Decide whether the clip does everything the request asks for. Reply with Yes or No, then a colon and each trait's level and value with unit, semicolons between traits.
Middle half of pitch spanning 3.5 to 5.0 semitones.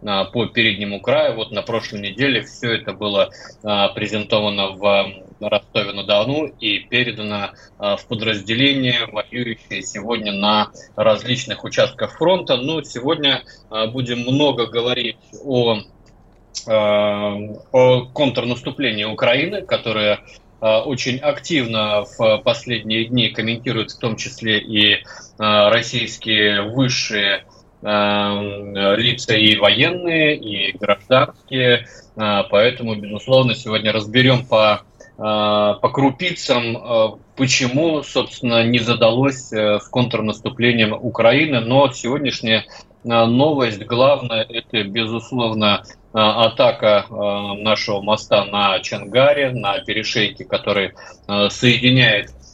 No: average, 3.1 semitones